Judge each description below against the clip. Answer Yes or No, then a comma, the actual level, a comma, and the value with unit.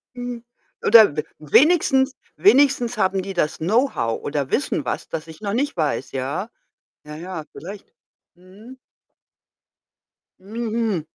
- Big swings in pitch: Yes, wide, 7.5 semitones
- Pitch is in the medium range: No, high, 195 Hz